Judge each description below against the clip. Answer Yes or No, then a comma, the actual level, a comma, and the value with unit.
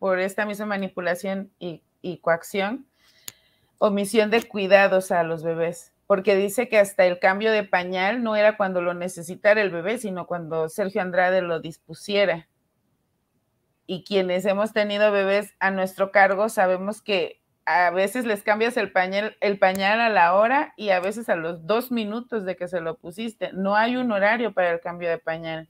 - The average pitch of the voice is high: Yes, high, 195 Hz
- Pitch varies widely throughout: No, average, 3.0 semitones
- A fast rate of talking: No, average, 175 wpm